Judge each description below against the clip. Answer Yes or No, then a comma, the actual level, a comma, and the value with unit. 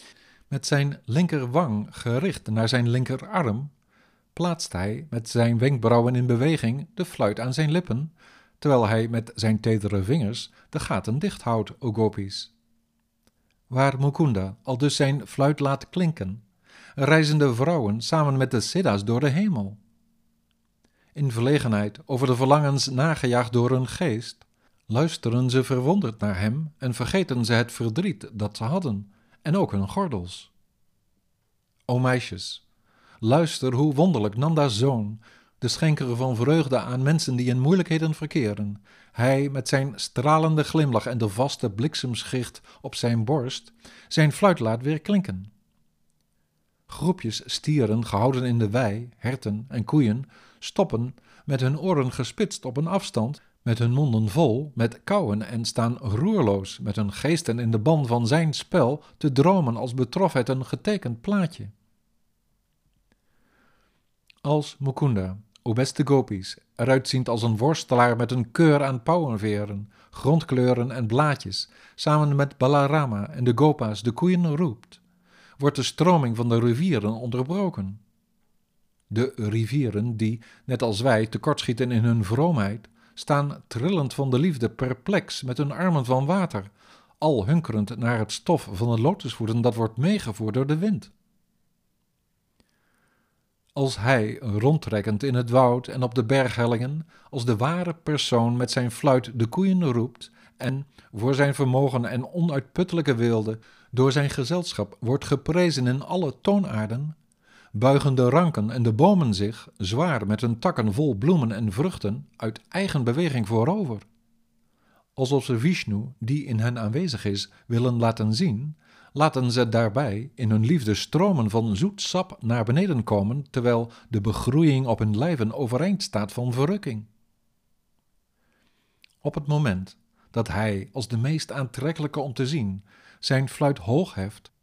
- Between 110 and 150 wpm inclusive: Yes, average, 145 wpm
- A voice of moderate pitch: No, low, 125 Hz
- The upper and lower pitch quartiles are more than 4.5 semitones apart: Yes, average, 4.9 semitones